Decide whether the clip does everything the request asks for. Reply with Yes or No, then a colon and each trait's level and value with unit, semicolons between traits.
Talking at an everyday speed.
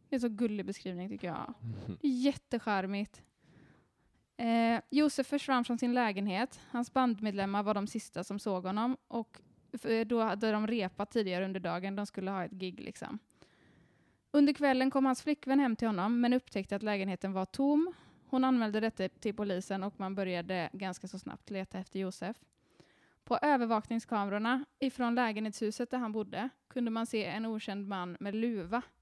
Yes: average, 165 wpm